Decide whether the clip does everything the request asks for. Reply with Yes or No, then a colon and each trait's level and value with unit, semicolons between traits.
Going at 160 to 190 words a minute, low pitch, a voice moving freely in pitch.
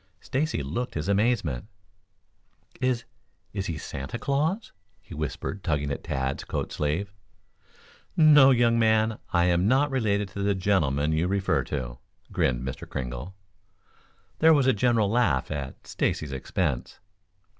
No: slow, 135 wpm; very low, 95 Hz; wide, 8.6 semitones